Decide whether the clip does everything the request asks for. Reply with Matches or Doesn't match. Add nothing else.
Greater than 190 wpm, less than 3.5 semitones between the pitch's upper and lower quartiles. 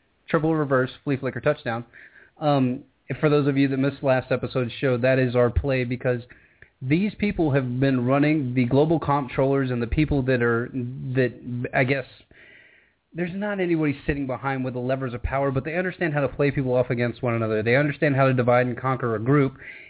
Matches